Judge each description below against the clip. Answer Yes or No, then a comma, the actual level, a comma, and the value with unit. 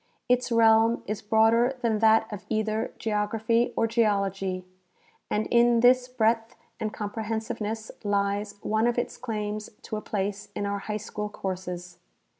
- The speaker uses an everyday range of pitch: No, narrow, 1.7 semitones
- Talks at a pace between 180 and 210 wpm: No, average, 150 wpm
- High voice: Yes, high, 220 Hz